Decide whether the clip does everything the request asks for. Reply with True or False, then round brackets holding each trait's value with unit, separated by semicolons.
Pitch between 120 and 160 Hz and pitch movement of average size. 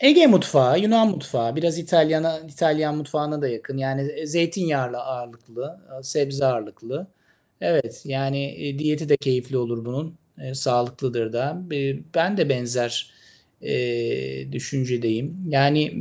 True (140 Hz; 4.1 semitones)